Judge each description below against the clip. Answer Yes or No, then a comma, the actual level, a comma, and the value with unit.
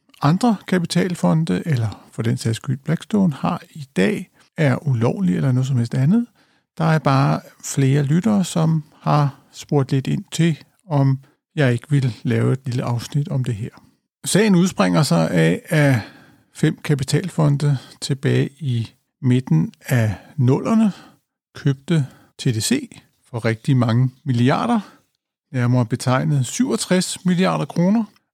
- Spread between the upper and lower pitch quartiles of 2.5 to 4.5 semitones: No, average, 5.1 semitones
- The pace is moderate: No, slow, 135 wpm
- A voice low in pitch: No, medium, 145 Hz